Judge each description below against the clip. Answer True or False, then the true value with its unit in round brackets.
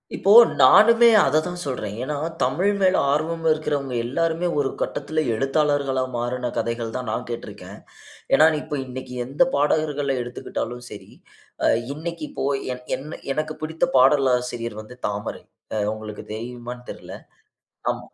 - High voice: False (135 Hz)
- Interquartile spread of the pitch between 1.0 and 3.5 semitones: False (4.1 semitones)